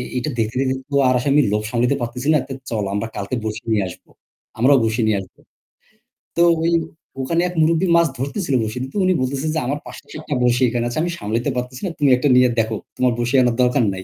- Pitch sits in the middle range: No, low, 125 Hz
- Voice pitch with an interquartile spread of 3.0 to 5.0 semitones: Yes, average, 3.6 semitones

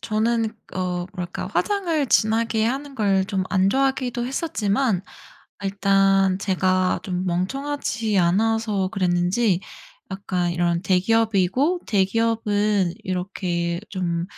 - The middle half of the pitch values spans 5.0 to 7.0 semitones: No, average, 3.7 semitones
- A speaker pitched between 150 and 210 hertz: Yes, high, 195 Hz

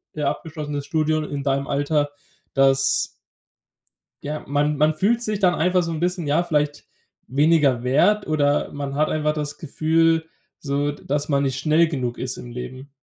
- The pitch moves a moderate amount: No, narrow, 2.3 semitones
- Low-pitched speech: No, medium, 150 Hz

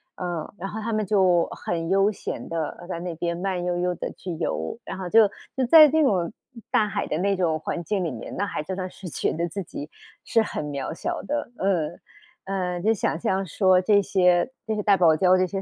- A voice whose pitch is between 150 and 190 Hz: Yes, medium, 185 Hz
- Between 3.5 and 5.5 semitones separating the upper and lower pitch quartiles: No, average, 2.8 semitones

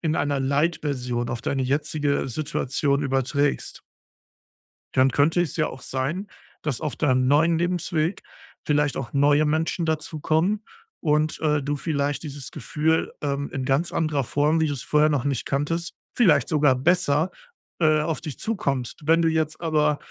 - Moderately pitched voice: Yes, medium, 150 Hz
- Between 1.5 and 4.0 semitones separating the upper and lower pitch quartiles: Yes, narrow, 2.4 semitones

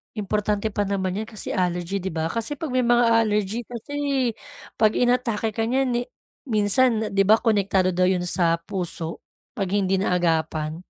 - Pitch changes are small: No, average, 3.7 semitones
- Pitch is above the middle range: Yes, high, 205 Hz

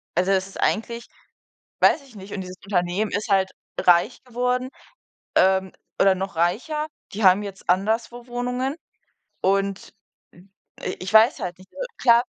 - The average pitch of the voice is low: No, high, 200 Hz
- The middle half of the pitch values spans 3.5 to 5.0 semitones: Yes, average, 4.0 semitones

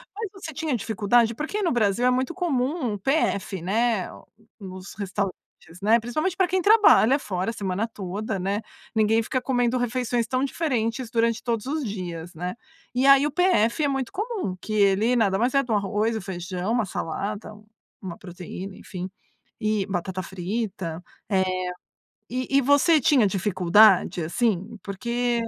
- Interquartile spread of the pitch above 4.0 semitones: Yes, average, 4.9 semitones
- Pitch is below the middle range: No, high, 220 Hz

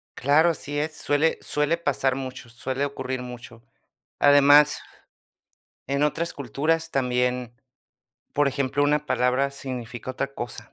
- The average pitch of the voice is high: No, medium, 140 Hz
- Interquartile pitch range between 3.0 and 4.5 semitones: No, narrow, 2.5 semitones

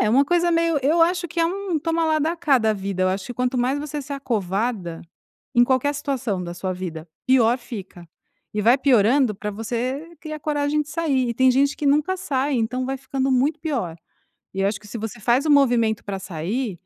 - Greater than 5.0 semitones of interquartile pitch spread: Yes, wide, 5.6 semitones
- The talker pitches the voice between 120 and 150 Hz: No, very high, 255 Hz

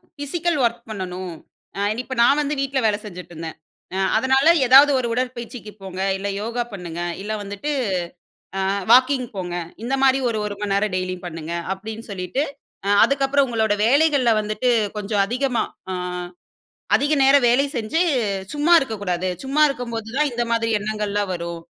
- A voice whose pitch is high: Yes, high, 230 Hz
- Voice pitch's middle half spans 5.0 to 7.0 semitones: Yes, average, 5.3 semitones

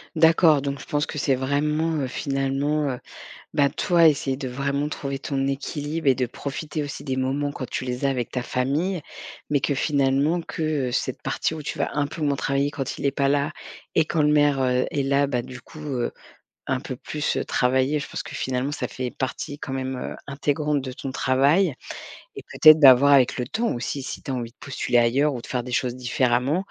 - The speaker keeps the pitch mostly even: Yes, narrow, 2.3 semitones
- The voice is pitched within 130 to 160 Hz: Yes, medium, 140 Hz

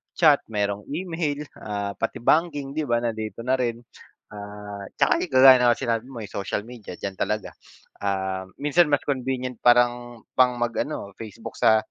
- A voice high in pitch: No, low, 120 Hz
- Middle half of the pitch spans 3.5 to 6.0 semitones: Yes, average, 4.5 semitones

